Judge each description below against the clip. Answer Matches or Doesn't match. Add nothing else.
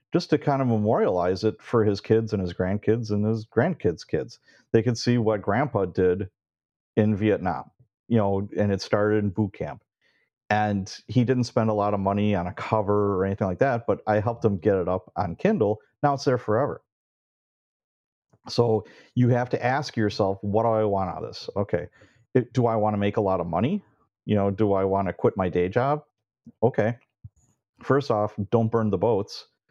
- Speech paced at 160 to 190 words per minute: Doesn't match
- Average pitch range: Matches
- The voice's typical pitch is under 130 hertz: Matches